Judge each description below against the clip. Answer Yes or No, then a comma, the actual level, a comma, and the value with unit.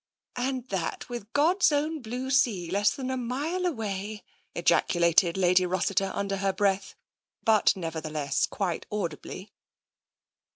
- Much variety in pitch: Yes, wide, 5.7 semitones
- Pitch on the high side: Yes, high, 205 Hz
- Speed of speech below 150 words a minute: Yes, slow, 135 wpm